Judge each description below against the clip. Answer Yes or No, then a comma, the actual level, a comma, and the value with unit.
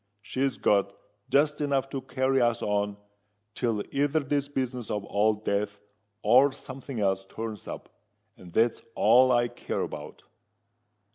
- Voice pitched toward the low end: Yes, low, 120 Hz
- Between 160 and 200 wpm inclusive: No, average, 145 wpm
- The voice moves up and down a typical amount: Yes, average, 4.6 semitones